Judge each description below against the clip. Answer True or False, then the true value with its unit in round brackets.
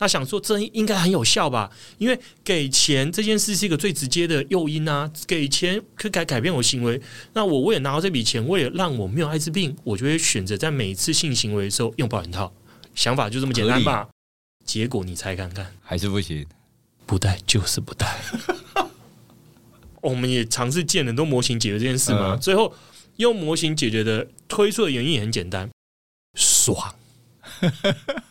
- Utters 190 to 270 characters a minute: False (280 characters per minute)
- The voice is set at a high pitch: False (130 Hz)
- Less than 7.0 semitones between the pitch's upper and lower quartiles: False (7.8 semitones)